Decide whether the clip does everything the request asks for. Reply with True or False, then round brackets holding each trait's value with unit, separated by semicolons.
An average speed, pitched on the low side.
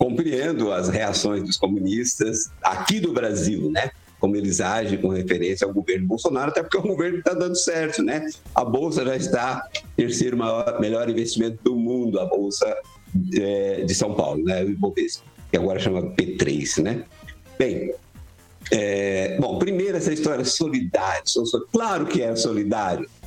True (160 wpm; 115 Hz)